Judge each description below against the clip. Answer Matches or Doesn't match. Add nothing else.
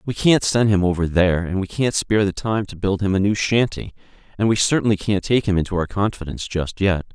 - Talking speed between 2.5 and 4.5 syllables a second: Doesn't match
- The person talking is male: Matches